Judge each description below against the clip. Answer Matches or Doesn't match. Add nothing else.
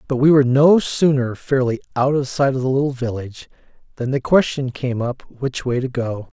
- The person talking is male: Matches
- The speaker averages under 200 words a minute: Doesn't match